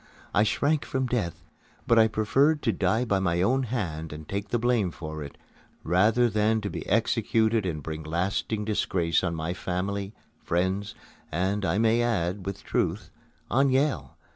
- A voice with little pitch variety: No, average, 4.7 semitones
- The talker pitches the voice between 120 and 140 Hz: No, low, 100 Hz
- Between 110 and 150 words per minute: No, average, 165 wpm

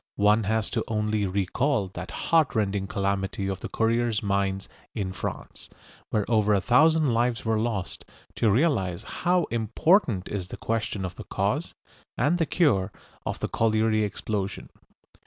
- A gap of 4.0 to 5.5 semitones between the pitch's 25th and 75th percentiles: No, average, 3.2 semitones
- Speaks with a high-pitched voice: No, low, 110 Hz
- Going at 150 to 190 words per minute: Yes, average, 155 wpm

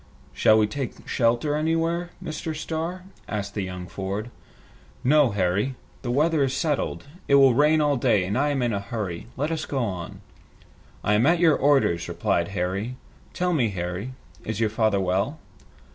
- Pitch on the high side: No, low, 120 Hz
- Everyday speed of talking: Yes, average, 170 wpm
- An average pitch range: No, wide, 6.9 semitones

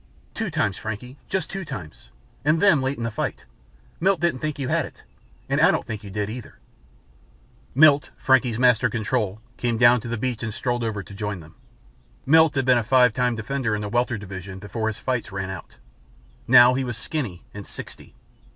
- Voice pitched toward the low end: Yes, low, 120 Hz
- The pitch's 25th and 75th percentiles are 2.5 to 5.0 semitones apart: Yes, average, 4.0 semitones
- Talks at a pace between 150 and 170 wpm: No, average, 200 wpm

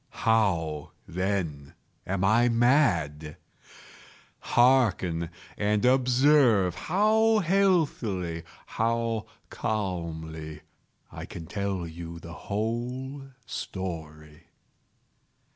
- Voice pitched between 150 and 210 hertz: No, low, 100 Hz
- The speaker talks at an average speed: No, slow, 70 wpm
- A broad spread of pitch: Yes, wide, 6.9 semitones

